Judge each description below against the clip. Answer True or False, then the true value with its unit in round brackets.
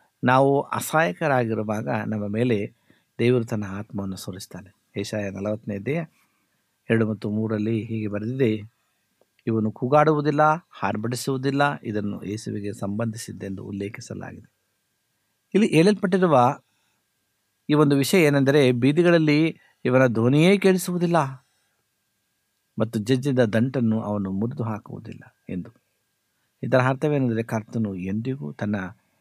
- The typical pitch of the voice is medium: False (115 Hz)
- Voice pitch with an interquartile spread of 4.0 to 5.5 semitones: True (4.4 semitones)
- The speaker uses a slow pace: False (90 wpm)